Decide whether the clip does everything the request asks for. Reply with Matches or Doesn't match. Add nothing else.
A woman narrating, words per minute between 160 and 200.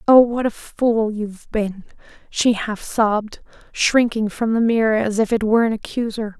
Matches